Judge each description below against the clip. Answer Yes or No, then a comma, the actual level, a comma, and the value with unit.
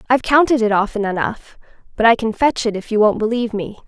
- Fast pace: Yes, fast, 230 wpm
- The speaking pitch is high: Yes, high, 225 Hz